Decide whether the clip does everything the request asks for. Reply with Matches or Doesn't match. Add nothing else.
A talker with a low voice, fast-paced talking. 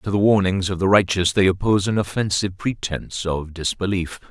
Doesn't match